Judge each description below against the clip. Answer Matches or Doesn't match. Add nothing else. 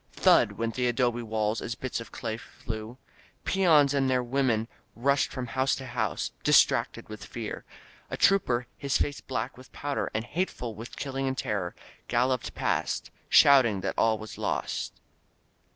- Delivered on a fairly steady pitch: Doesn't match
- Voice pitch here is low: Matches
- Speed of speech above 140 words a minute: Matches